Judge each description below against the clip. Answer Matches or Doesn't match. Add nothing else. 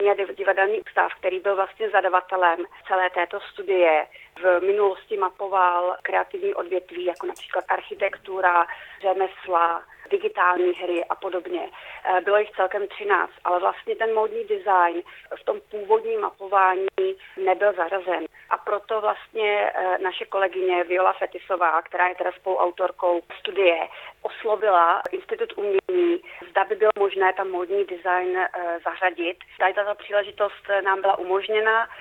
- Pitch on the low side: Doesn't match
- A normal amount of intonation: Matches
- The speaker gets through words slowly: Doesn't match